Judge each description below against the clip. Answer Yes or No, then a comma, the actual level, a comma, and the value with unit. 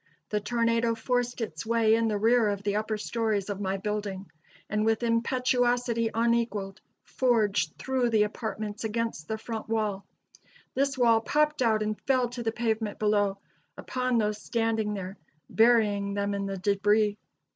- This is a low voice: No, high, 220 Hz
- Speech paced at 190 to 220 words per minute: No, average, 155 wpm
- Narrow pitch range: Yes, narrow, 2.2 semitones